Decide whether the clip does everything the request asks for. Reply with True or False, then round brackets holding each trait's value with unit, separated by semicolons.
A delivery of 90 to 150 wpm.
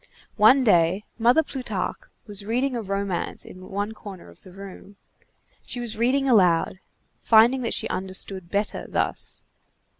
True (145 wpm)